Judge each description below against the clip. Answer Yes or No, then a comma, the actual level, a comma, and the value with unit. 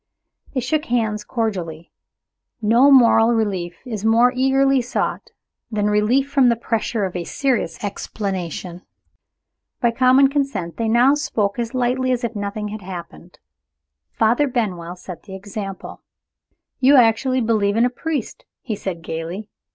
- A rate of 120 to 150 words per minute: Yes, average, 145 wpm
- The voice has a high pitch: Yes, high, 225 Hz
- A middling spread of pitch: Yes, average, 4.2 semitones